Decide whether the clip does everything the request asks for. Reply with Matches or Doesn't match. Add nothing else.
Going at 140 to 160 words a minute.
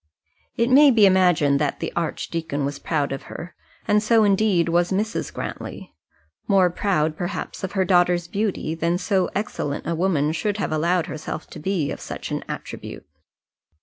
Doesn't match